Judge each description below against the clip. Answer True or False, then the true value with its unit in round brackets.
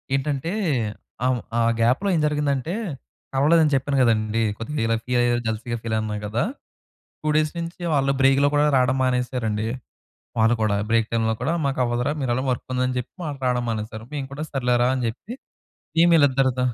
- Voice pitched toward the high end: False (125 Hz)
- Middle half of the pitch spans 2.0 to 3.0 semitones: False (3.6 semitones)